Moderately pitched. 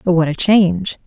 Yes: medium, 180 Hz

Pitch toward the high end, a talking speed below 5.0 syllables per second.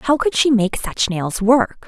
Yes: high, 235 Hz; 3.9 syllables/s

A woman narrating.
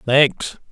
No: male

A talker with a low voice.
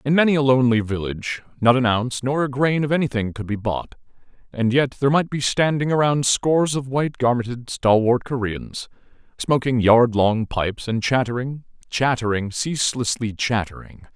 Yes: low, 125 Hz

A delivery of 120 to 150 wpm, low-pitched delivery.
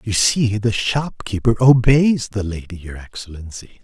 Yes: average, 140 wpm; low, 110 Hz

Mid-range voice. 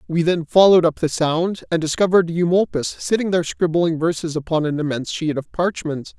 Yes: medium, 165 Hz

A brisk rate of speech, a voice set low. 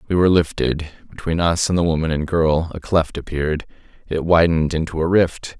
No: average, 195 wpm; very low, 80 Hz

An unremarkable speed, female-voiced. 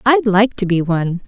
No: fast, 235 wpm; female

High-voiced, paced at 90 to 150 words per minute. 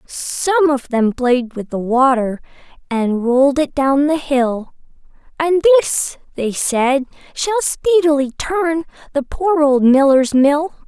Yes: very high, 280 Hz; average, 140 wpm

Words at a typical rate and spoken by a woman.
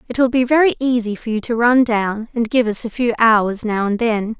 No: fast, 260 wpm; female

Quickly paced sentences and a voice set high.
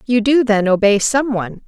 Yes: fast, 215 wpm; high, 225 Hz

